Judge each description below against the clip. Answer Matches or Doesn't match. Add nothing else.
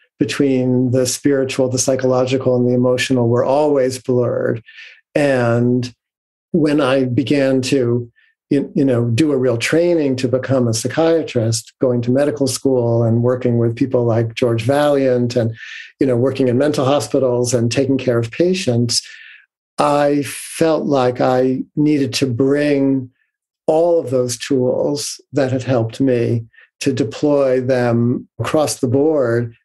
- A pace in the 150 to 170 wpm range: Doesn't match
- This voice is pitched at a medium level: Doesn't match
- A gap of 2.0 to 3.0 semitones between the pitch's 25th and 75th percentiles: Matches